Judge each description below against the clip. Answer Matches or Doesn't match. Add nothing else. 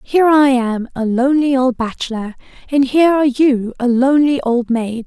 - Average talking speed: Matches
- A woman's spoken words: Matches